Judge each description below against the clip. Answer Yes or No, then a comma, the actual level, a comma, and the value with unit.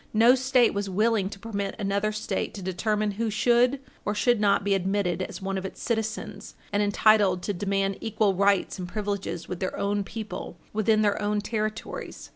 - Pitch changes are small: Yes, narrow, 1.8 semitones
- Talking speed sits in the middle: Yes, average, 185 wpm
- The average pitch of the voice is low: No, high, 205 Hz